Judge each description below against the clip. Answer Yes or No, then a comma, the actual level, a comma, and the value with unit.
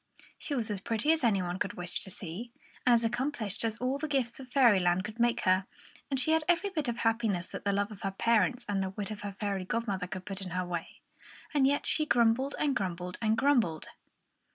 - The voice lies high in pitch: Yes, high, 220 Hz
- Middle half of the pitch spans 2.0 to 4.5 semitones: No, average, 4.9 semitones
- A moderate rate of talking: No, fast, 230 wpm